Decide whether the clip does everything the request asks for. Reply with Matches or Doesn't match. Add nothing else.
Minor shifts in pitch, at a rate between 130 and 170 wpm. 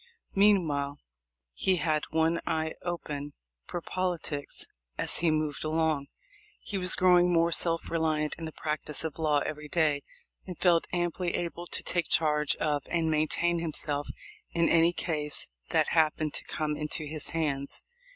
Matches